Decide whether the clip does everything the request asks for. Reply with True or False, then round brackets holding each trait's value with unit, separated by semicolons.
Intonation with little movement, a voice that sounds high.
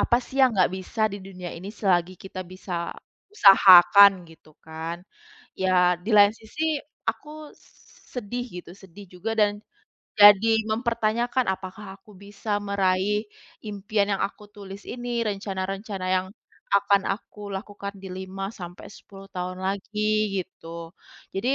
True (1.9 semitones; 195 Hz)